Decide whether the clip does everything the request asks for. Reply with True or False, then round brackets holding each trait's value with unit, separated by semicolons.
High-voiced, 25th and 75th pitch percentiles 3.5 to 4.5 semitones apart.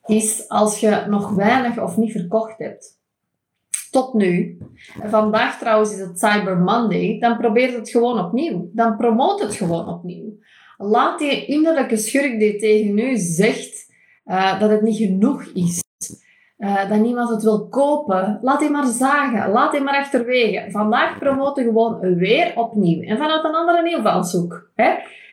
True (220 Hz; 3.8 semitones)